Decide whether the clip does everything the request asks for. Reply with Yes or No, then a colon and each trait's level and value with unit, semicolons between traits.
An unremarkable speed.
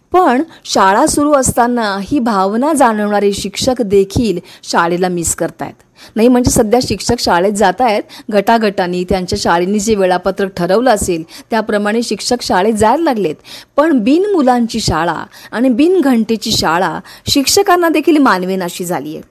No: fast, 135 wpm